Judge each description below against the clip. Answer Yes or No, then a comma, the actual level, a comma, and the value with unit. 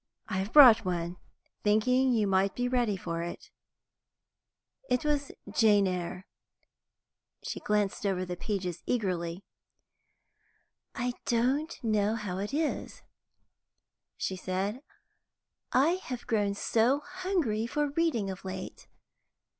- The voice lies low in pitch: No, high, 215 Hz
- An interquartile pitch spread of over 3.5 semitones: Yes, average, 4.9 semitones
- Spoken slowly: Yes, slow, 115 wpm